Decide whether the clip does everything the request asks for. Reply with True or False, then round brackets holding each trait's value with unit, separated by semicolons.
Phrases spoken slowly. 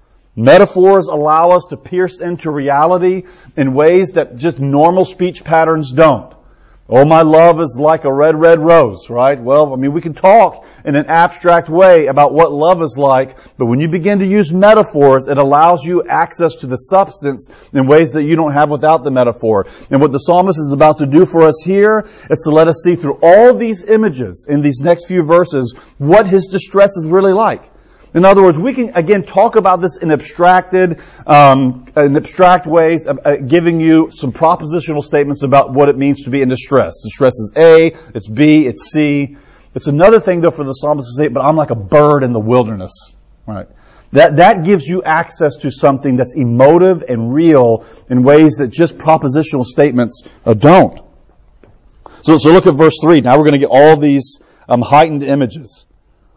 False (195 wpm)